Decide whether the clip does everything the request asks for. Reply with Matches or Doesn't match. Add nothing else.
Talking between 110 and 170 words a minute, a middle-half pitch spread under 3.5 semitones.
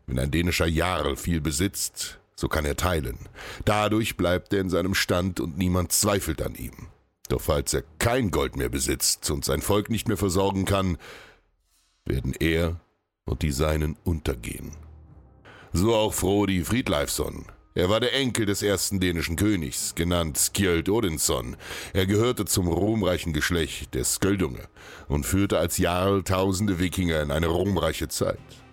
Doesn't match